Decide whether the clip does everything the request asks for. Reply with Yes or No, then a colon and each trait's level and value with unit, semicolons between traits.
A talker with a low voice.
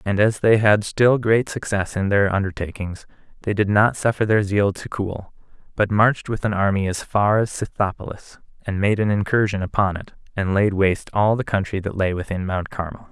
Yes: low, 100 Hz